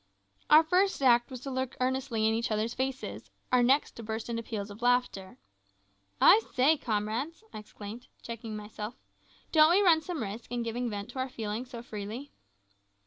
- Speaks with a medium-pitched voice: No, high, 240 Hz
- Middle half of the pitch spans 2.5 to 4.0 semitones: Yes, average, 3.3 semitones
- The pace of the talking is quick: No, average, 180 wpm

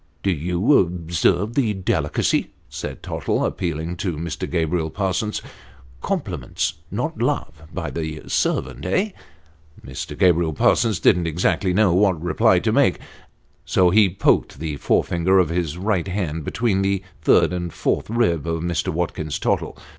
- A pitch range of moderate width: Yes, average, 3.2 semitones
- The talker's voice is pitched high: No, very low, 90 Hz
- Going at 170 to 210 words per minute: No, average, 150 wpm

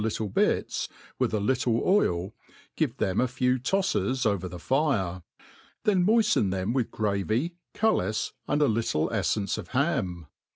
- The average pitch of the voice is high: No, low, 115 Hz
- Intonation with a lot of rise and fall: Yes, wide, 6.4 semitones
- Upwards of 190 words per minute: No, average, 150 wpm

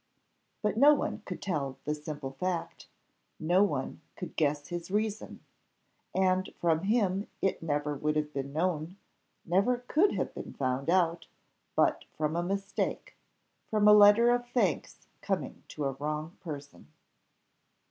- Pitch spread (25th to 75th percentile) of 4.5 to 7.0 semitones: Yes, average, 5.2 semitones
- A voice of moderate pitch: Yes, medium, 170 Hz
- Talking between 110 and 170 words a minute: Yes, average, 145 wpm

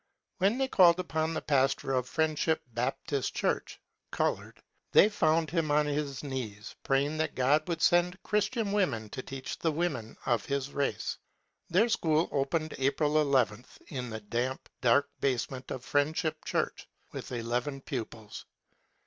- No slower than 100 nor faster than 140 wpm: No, average, 150 wpm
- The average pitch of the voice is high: No, medium, 145 Hz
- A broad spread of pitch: No, average, 4.0 semitones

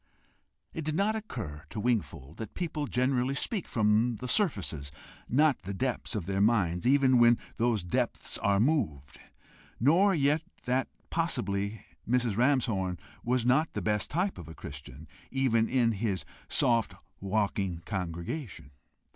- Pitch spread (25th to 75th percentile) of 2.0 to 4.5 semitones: No, wide, 5.6 semitones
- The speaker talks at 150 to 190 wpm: No, average, 140 wpm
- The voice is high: No, low, 115 Hz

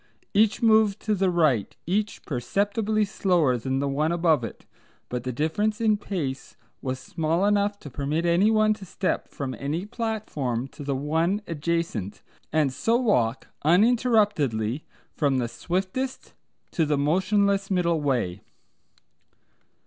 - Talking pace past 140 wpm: No, slow, 135 wpm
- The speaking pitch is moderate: Yes, medium, 170 Hz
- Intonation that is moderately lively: No, wide, 6.8 semitones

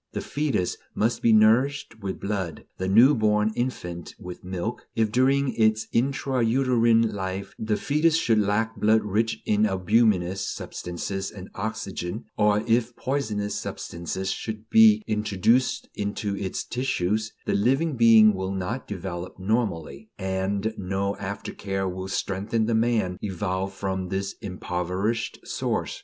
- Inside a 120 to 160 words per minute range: Yes, average, 140 wpm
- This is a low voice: Yes, low, 105 Hz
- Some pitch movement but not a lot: Yes, average, 3.2 semitones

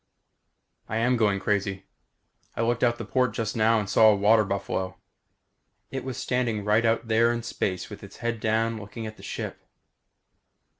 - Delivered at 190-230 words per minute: No, average, 180 wpm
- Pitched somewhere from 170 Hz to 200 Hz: No, low, 110 Hz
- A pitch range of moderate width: No, narrow, 2.1 semitones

